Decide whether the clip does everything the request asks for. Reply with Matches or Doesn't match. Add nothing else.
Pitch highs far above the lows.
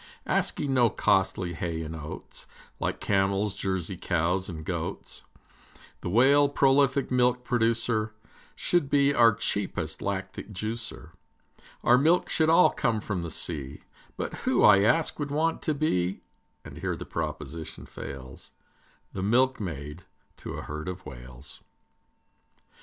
Matches